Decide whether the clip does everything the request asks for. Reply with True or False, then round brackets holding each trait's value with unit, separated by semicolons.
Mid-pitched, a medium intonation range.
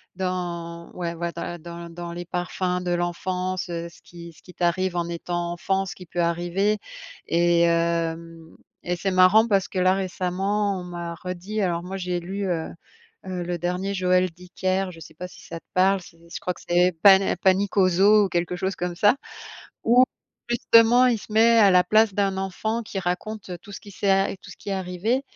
False (180 Hz; 2.0 semitones)